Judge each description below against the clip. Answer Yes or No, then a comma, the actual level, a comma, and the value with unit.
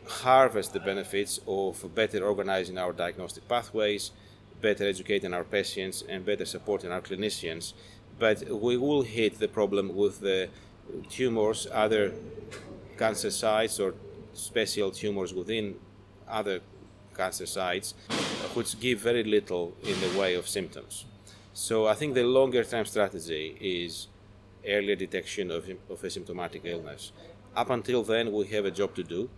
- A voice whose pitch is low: Yes, low, 100 Hz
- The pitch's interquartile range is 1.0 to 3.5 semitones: Yes, narrow, 2.5 semitones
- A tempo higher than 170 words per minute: No, average, 140 wpm